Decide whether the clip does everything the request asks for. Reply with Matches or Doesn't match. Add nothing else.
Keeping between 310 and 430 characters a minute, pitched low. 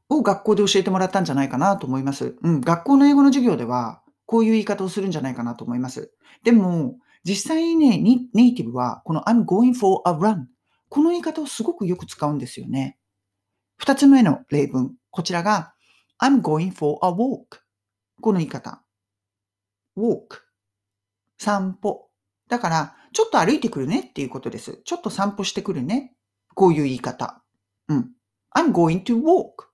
Doesn't match